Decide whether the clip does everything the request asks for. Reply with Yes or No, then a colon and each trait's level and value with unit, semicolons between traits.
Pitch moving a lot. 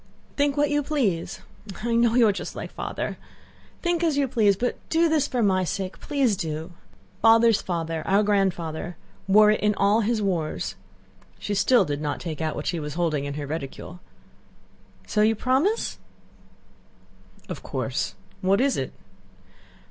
Yes: wide, 6.6 semitones